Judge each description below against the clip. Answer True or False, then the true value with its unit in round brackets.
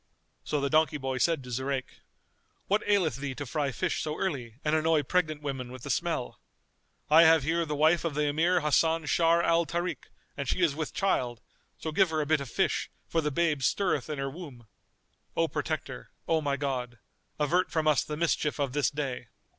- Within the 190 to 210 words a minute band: True (200 wpm)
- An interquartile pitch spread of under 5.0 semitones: True (3.0 semitones)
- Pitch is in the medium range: True (150 Hz)